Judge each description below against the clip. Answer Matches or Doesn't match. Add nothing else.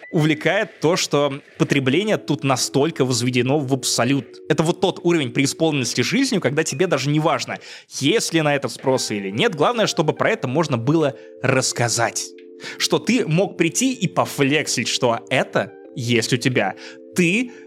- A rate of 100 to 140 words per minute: Doesn't match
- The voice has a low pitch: Doesn't match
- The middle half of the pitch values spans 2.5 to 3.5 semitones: Doesn't match